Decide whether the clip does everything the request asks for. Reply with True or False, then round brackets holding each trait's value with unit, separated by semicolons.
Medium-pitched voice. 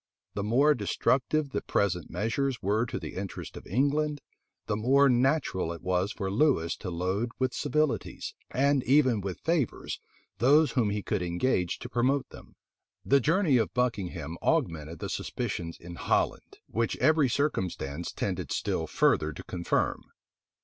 False (115 Hz)